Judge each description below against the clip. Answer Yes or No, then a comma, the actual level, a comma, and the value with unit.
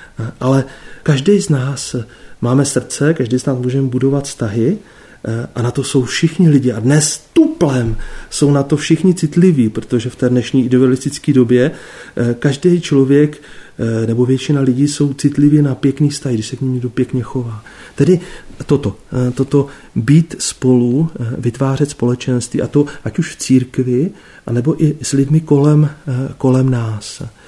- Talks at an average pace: Yes, average, 150 wpm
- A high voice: No, low, 135 Hz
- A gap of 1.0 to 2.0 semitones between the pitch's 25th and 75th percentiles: No, average, 2.8 semitones